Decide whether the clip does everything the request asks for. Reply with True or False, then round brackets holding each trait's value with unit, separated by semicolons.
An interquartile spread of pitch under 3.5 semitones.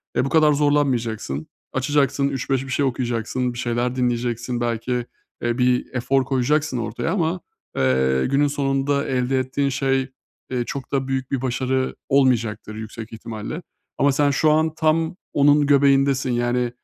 True (2.7 semitones)